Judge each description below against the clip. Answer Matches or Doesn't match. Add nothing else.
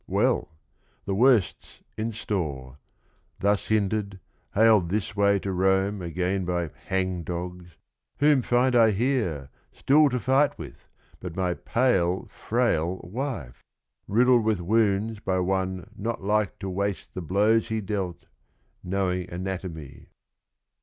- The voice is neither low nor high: Doesn't match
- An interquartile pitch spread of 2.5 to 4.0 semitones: Matches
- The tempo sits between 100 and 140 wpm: Matches